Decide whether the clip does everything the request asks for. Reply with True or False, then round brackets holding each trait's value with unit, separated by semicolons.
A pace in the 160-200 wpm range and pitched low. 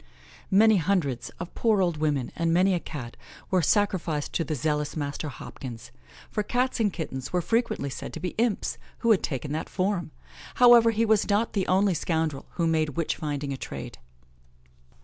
False (180 wpm; 170 Hz)